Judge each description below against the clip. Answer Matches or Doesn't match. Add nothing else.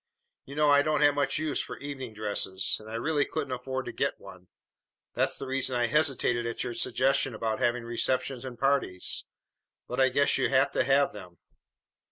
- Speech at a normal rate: Matches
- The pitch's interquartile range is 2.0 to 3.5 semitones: Matches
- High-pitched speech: Doesn't match